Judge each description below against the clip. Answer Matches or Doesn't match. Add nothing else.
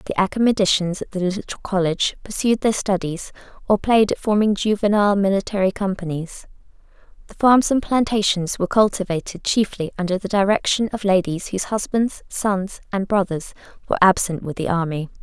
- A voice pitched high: Matches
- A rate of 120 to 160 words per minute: Matches